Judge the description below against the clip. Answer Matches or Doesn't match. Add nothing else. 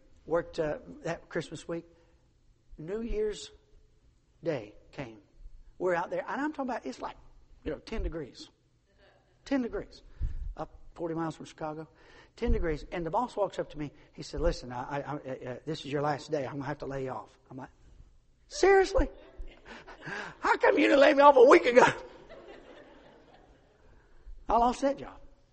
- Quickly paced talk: Doesn't match